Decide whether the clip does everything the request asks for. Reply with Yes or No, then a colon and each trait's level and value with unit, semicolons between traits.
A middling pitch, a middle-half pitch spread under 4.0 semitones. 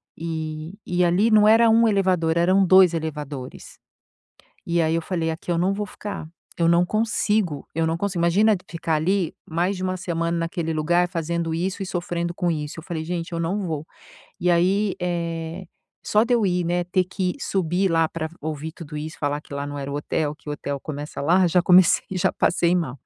Yes: medium, 170 Hz; narrow, 2.5 semitones